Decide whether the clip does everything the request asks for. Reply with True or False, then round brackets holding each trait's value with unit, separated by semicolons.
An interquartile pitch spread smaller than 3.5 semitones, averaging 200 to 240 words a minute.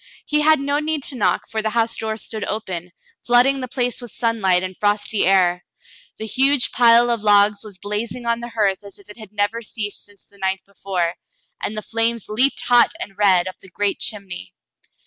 True (3.1 semitones; 205 wpm)